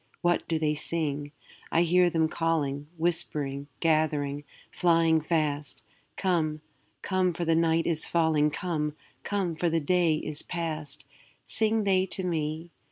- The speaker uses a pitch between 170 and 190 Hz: No, medium, 160 Hz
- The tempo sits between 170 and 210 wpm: No, average, 140 wpm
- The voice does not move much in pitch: Yes, narrow, 2.3 semitones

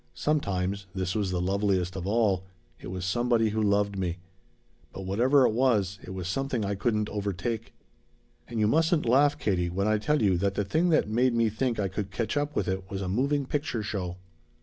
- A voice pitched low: Yes, low, 105 Hz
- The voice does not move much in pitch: No, average, 4.2 semitones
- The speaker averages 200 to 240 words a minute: Yes, fast, 205 wpm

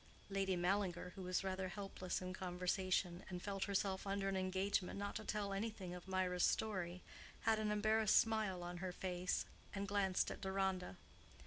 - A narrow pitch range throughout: Yes, narrow, 1.7 semitones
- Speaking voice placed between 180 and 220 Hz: Yes, high, 190 Hz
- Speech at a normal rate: Yes, average, 170 wpm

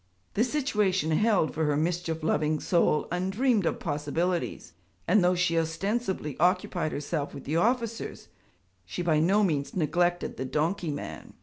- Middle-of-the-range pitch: Yes, medium, 175 Hz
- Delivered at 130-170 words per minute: Yes, average, 145 wpm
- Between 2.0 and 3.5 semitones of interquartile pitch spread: No, average, 3.9 semitones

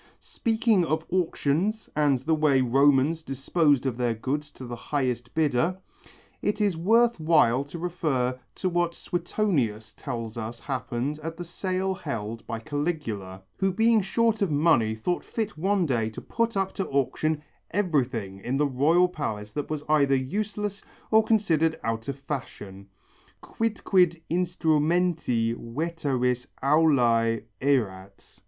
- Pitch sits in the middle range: Yes, medium, 150 Hz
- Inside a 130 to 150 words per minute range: Yes, average, 140 wpm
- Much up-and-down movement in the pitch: Yes, wide, 6.3 semitones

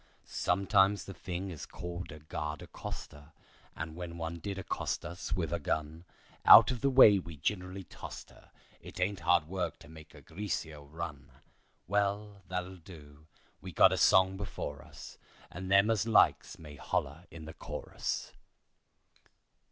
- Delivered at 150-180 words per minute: Yes, average, 160 wpm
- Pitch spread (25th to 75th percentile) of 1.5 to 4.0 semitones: Yes, average, 3.6 semitones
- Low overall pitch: Yes, very low, 85 Hz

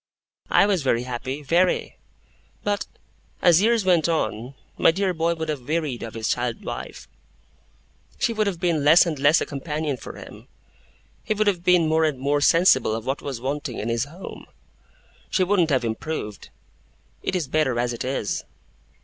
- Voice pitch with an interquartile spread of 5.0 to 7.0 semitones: Yes, average, 5.3 semitones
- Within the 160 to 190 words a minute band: Yes, average, 175 wpm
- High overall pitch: No, medium, 155 Hz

